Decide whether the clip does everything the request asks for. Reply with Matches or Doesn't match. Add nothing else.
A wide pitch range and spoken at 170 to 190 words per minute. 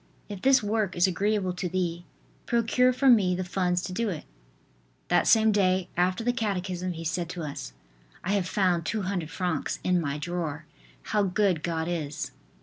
Doesn't match